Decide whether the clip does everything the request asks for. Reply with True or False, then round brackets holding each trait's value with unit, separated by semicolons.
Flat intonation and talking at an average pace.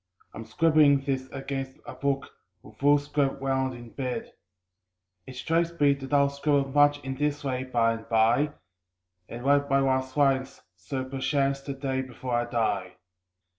True (1.5 semitones; 160 wpm)